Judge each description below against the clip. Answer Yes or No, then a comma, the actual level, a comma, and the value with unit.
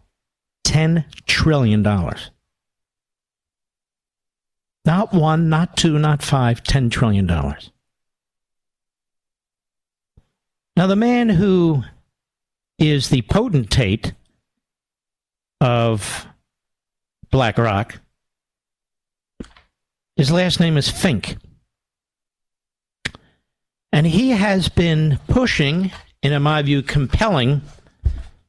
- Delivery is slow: Yes, slow, 70 wpm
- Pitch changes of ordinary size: No, wide, 6.1 semitones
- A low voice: No, medium, 145 Hz